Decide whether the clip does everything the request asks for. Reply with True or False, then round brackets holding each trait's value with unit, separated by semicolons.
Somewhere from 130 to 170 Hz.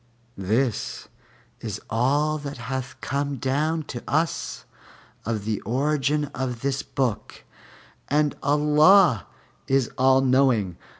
True (135 Hz)